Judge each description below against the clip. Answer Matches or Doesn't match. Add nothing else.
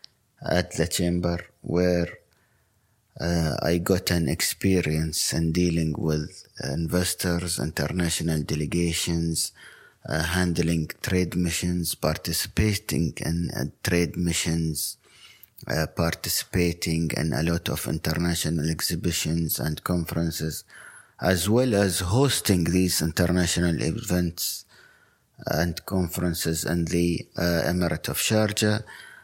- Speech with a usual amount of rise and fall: Doesn't match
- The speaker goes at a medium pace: Doesn't match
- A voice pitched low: Matches